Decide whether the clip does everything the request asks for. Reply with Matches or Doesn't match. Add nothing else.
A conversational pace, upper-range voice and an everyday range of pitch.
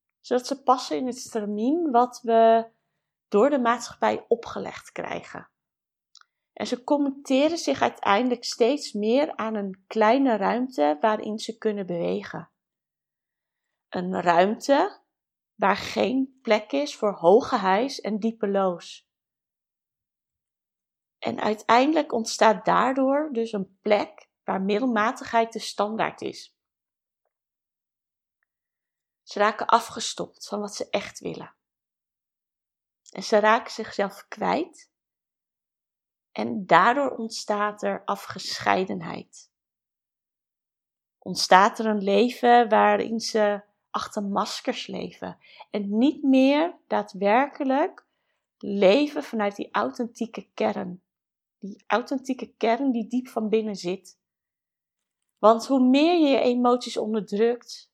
Doesn't match